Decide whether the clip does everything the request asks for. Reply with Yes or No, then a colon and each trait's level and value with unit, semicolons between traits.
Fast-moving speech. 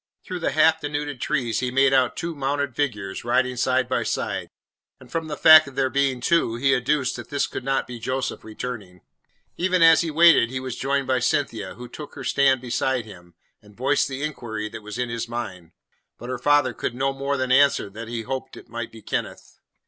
Yes: fast, 215 wpm